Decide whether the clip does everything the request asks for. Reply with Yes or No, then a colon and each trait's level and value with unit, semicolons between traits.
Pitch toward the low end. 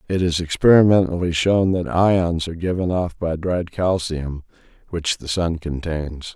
Yes: very low, 85 Hz